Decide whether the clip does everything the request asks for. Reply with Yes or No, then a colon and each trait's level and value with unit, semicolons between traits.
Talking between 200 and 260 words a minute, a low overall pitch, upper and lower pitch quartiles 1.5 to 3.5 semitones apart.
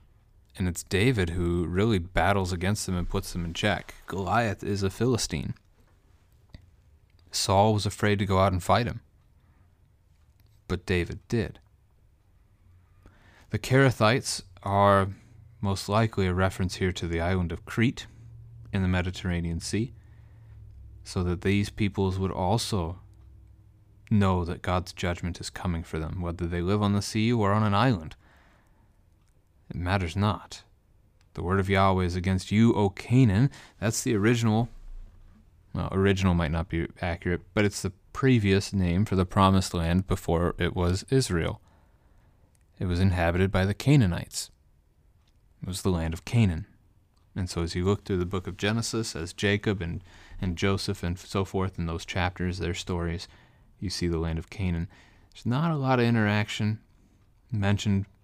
No: average, 155 wpm; very low, 95 Hz; average, 2.7 semitones